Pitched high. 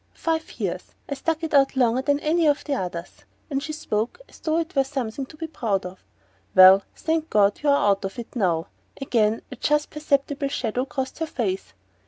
Yes: very high, 270 Hz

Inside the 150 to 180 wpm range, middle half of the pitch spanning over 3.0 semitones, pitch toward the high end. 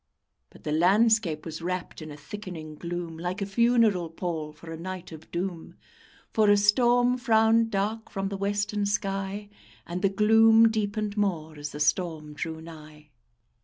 Yes: average, 165 wpm; average, 4.5 semitones; high, 195 Hz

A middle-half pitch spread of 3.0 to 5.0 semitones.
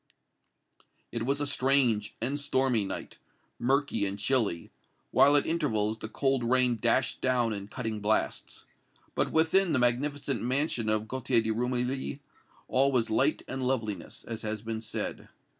Yes: average, 3.7 semitones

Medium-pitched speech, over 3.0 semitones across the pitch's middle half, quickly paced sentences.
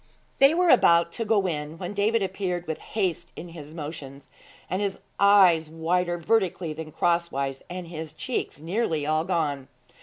No: medium, 170 Hz; average, 3.6 semitones; average, 155 wpm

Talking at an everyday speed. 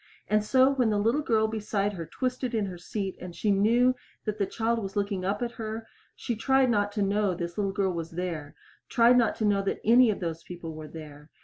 No: fast, 230 wpm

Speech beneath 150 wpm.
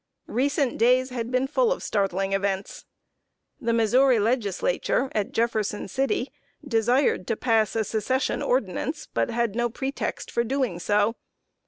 Yes: average, 140 wpm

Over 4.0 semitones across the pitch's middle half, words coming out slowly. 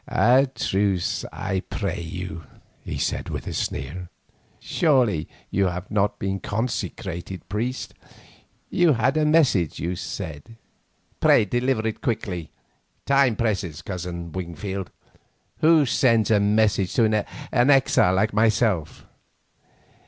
Yes: average, 4.8 semitones; slow, 115 wpm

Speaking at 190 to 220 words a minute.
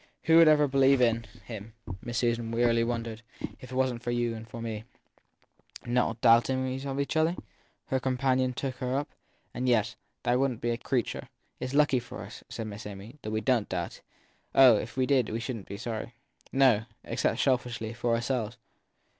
Yes: average, 195 wpm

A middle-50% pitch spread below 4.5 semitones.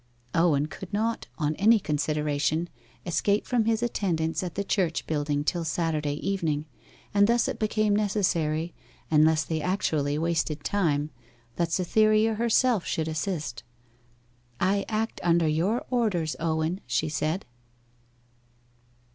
No: average, 4.8 semitones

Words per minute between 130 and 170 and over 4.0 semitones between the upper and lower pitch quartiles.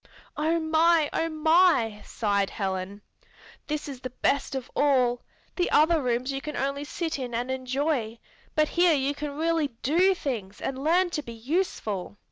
Yes: average, 165 wpm; average, 4.7 semitones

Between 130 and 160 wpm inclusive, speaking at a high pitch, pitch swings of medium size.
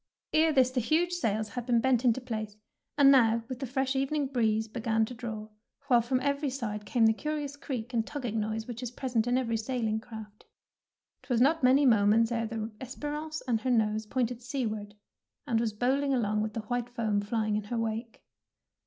No: average, 200 wpm; high, 235 Hz; average, 3.1 semitones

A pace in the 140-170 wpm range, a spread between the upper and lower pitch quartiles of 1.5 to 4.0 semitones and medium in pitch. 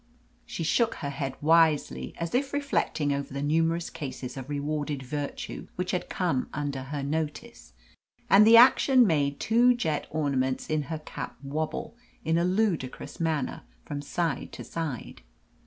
Yes: average, 155 wpm; average, 3.5 semitones; medium, 155 Hz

